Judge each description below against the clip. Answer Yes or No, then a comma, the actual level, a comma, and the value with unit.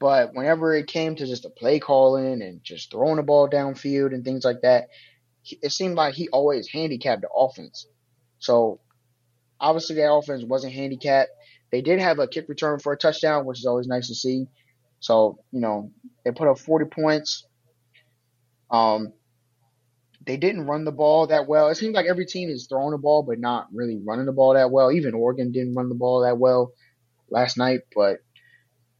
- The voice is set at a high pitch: No, low, 130 Hz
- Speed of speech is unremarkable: Yes, average, 190 wpm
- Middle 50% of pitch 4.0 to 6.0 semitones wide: No, average, 3.6 semitones